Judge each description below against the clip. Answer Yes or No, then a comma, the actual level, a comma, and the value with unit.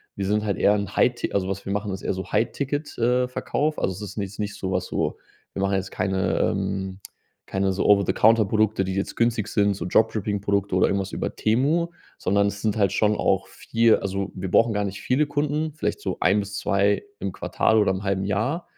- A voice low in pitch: Yes, low, 100 Hz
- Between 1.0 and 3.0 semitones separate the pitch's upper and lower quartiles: Yes, narrow, 2.4 semitones